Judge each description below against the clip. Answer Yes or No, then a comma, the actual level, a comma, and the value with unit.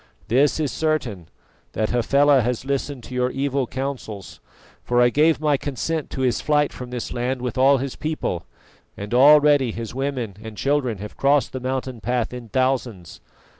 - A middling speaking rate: Yes, average, 170 wpm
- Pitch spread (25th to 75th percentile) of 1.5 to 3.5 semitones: Yes, average, 2.8 semitones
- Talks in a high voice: No, low, 130 Hz